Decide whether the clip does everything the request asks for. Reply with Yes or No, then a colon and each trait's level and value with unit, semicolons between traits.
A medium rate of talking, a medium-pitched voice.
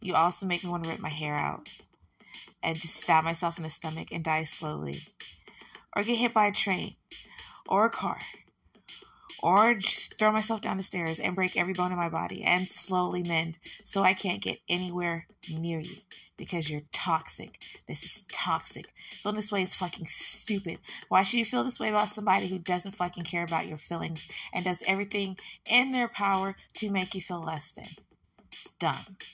Yes: average, 190 wpm; medium, 180 Hz